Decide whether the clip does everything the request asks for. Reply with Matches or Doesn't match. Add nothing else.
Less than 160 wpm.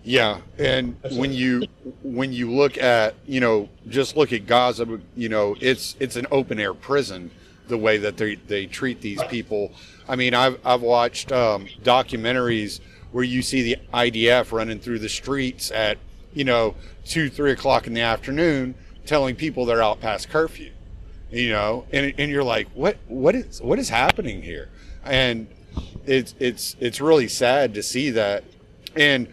Doesn't match